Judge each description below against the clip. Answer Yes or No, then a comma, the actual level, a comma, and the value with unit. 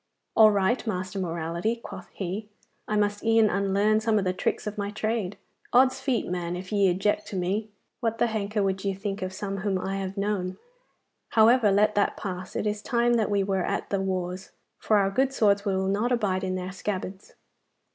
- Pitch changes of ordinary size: No, narrow, 2.3 semitones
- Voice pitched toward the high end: Yes, high, 200 Hz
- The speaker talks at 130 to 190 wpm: No, average, 200 wpm